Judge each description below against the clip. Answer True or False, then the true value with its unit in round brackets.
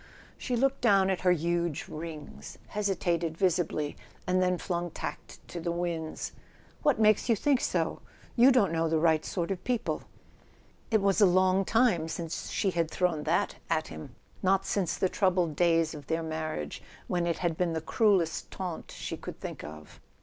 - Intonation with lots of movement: False (3.1 semitones)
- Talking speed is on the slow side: False (180 wpm)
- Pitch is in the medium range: True (175 Hz)